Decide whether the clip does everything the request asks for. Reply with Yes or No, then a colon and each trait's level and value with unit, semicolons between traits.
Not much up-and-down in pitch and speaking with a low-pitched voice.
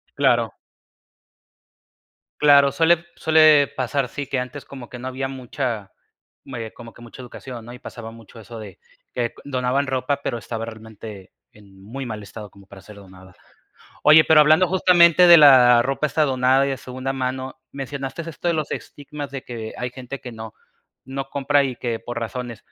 No: average, 3.4 semitones; low, 130 Hz